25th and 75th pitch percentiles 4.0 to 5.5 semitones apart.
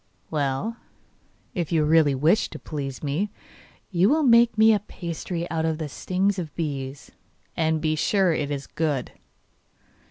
Yes: average, 4.5 semitones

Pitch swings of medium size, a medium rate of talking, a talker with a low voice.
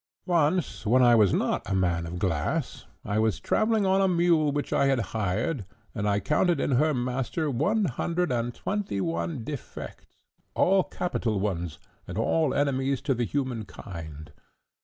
No: wide, 7.8 semitones; average, 165 wpm; low, 125 Hz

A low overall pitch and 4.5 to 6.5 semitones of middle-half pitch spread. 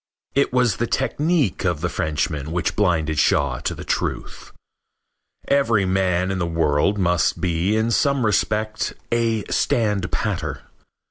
Yes: very low, 95 Hz; average, 5.0 semitones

